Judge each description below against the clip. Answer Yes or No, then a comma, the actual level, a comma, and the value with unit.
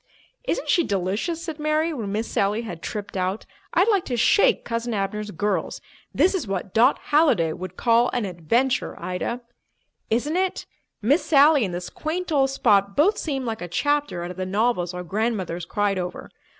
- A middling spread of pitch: No, wide, 7.5 semitones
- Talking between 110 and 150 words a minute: No, average, 180 wpm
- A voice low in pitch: No, high, 225 Hz